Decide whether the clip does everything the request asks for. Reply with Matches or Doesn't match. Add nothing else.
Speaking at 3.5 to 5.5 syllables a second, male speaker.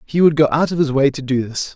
Doesn't match